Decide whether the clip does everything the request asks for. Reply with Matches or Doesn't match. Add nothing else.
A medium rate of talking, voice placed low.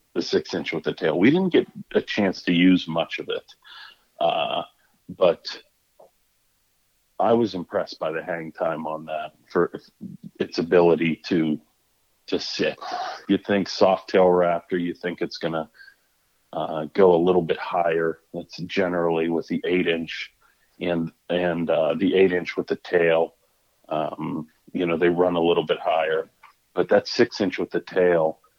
Matches